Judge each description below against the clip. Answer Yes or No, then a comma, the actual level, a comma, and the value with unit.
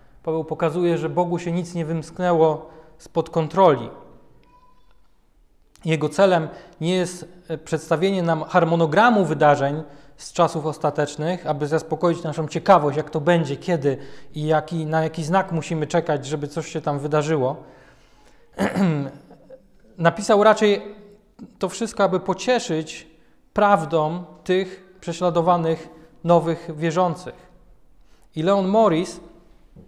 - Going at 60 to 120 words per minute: Yes, slow, 110 wpm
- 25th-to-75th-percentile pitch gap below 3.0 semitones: Yes, narrow, 2.6 semitones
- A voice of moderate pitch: Yes, medium, 165 Hz